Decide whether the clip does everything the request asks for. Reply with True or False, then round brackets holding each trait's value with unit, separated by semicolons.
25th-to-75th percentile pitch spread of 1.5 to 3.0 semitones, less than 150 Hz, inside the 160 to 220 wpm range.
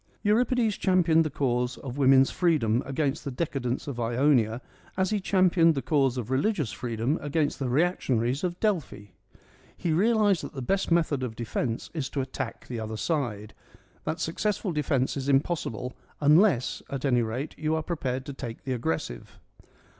False (5.3 semitones; 140 Hz; 170 wpm)